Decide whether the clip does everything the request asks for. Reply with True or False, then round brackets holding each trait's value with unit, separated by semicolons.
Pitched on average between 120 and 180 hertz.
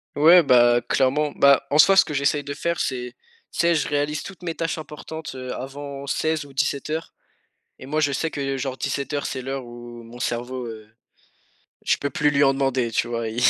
True (140 Hz)